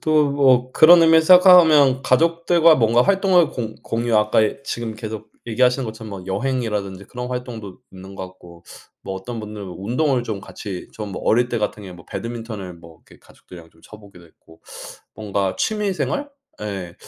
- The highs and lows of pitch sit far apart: Yes, wide, 5.7 semitones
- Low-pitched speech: Yes, low, 115 Hz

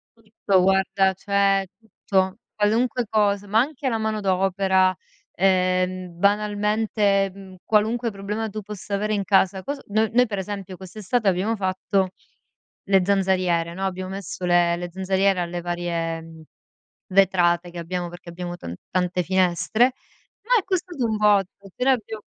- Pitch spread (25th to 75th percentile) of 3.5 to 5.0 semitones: No, narrow, 2.5 semitones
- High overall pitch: Yes, high, 195 Hz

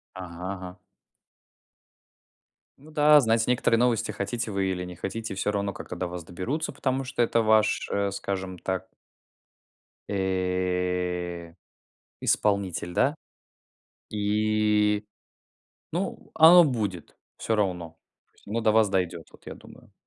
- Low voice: Yes, low, 100 Hz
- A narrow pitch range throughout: No, average, 3.7 semitones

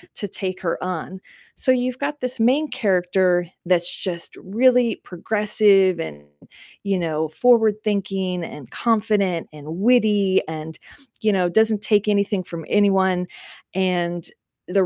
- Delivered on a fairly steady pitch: No, average, 3.5 semitones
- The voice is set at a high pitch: Yes, high, 195 Hz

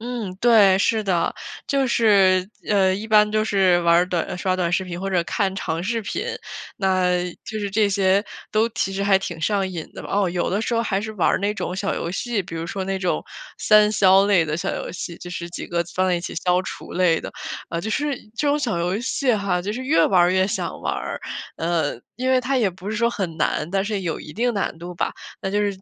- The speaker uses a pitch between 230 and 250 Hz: No, high, 195 Hz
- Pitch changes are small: No, average, 3.1 semitones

